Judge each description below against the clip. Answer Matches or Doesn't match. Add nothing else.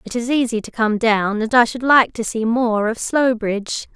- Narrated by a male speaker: Doesn't match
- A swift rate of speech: Matches